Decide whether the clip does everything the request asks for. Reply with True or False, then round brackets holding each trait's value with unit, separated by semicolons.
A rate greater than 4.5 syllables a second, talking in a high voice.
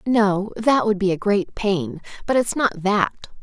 False (4.1 syllables/s; 200 Hz)